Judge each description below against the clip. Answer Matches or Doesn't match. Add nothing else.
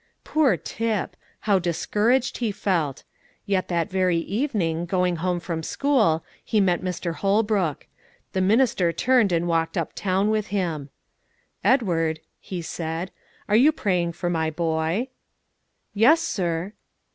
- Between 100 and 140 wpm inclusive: Matches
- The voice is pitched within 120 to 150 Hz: Doesn't match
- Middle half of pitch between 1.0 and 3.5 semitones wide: Doesn't match